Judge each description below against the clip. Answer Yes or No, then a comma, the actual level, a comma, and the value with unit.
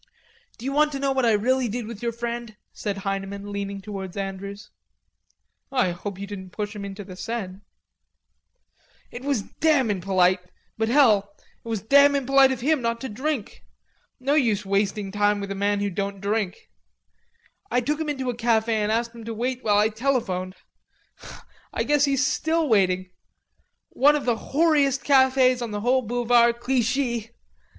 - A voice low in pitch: No, high, 230 Hz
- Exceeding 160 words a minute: Yes, average, 170 wpm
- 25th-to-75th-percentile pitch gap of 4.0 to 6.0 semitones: Yes, average, 4.6 semitones